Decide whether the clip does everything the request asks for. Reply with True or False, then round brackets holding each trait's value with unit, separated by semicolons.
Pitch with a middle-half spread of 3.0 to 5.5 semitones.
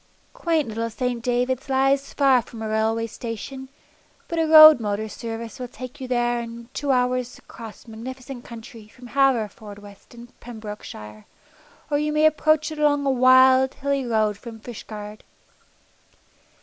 True (3.3 semitones)